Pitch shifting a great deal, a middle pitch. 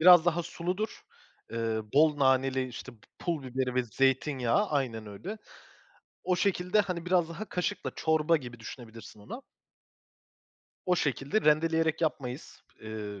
Yes: wide, 5.9 semitones; medium, 150 Hz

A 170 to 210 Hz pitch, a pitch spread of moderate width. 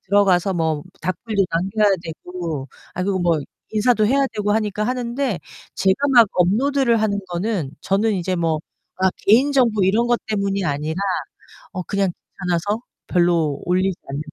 Yes: high, 195 Hz; average, 3.9 semitones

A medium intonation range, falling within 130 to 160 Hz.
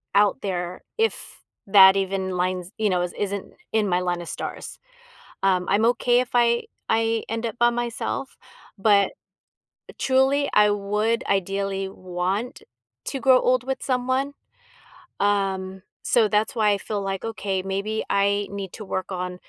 No: average, 3.3 semitones; high, 200 Hz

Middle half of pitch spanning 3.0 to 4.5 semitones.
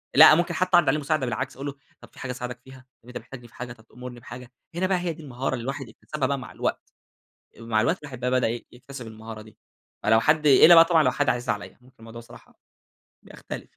Yes: average, 3.9 semitones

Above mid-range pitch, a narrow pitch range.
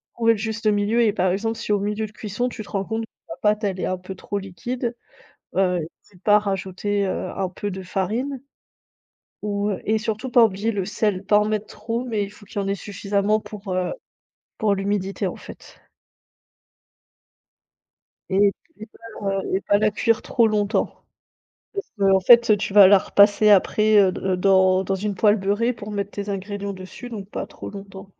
Yes: high, 205 Hz; narrow, 1.8 semitones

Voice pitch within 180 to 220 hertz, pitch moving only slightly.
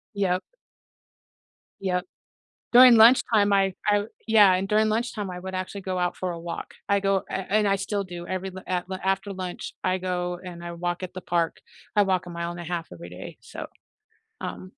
Yes: medium, 185 Hz; narrow, 2.1 semitones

